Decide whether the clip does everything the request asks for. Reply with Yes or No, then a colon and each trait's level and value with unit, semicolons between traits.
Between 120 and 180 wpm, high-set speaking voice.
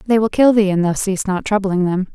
No: fast, 280 wpm; high, 200 Hz